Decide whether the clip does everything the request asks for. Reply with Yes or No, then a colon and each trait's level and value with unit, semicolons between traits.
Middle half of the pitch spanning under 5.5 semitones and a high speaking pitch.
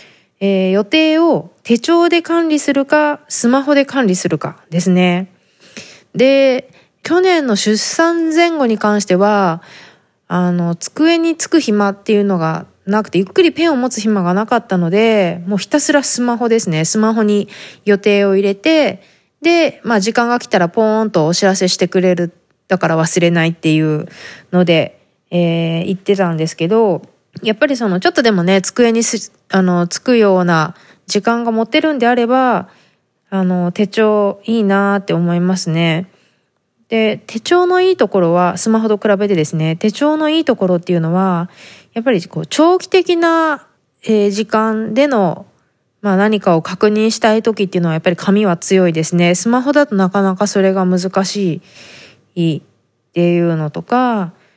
Yes: average, 5.1 semitones; high, 205 Hz